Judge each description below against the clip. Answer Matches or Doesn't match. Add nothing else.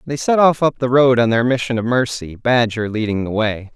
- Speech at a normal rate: Doesn't match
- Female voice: Doesn't match